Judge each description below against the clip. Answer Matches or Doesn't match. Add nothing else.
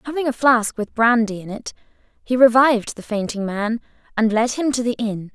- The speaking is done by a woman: Matches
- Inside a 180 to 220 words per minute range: Matches